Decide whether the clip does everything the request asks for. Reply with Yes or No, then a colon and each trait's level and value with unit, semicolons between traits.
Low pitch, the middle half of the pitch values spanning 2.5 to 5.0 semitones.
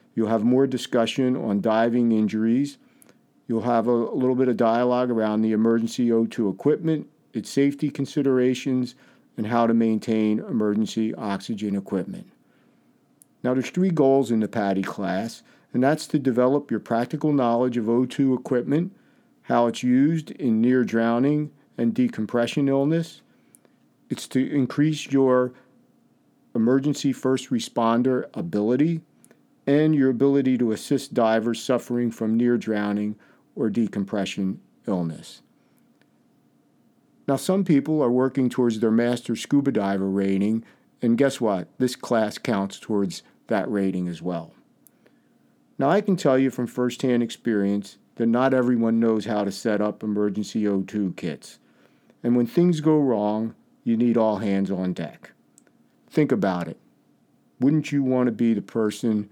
Yes: low, 120 Hz; average, 3.7 semitones